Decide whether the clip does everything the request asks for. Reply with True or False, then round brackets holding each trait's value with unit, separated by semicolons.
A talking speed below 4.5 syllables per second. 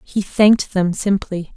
True (4.1 syllables/s)